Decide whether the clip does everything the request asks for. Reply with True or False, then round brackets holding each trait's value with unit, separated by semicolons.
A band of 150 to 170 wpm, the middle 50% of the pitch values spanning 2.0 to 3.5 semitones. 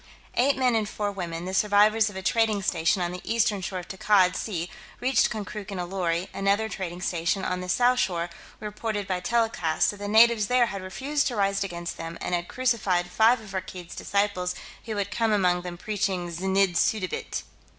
False (195 wpm; 3.2 semitones)